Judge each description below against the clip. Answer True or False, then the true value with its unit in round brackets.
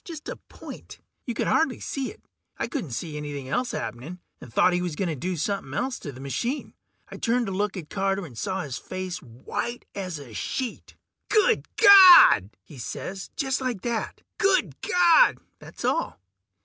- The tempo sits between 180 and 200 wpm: True (185 wpm)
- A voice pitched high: True (195 Hz)